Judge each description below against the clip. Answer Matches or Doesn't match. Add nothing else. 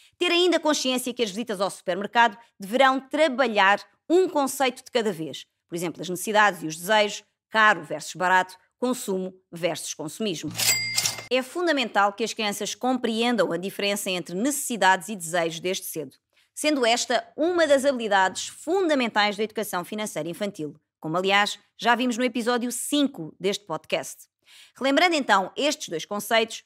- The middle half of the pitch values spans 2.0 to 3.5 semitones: Doesn't match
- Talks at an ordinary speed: Matches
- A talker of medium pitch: Doesn't match